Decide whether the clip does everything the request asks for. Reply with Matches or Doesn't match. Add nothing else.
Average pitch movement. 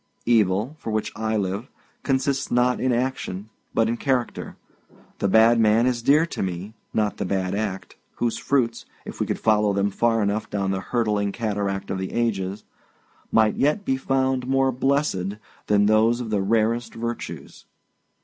Matches